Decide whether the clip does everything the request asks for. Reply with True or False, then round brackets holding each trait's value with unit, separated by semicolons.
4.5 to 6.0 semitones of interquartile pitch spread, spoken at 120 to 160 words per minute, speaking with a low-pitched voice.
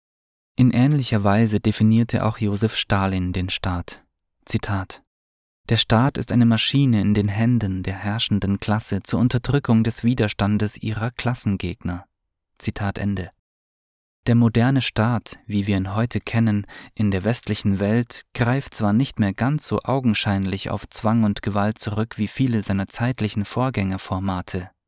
False (2.8 semitones; 140 wpm; 105 Hz)